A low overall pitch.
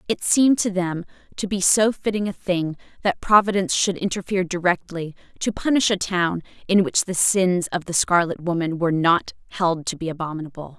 No: medium, 180 Hz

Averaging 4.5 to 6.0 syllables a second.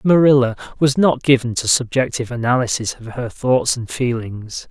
Yes: 5.0 syllables/s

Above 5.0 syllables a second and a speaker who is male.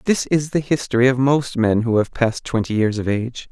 Yes: 5.6 syllables/s; male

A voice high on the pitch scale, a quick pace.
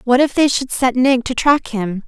Yes: very high, 255 Hz; fast, 260 wpm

